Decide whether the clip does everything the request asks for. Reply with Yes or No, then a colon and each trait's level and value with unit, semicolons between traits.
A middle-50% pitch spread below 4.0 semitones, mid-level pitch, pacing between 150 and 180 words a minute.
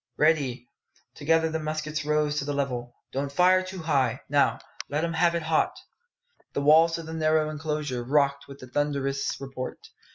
Yes: narrow, 2.4 semitones; medium, 150 Hz; average, 170 wpm